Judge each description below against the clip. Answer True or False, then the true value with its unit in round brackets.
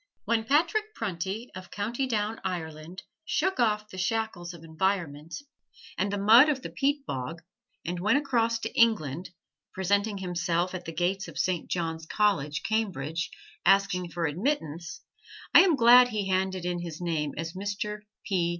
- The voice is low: False (190 Hz)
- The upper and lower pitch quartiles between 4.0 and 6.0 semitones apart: True (4.7 semitones)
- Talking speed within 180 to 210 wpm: False (160 wpm)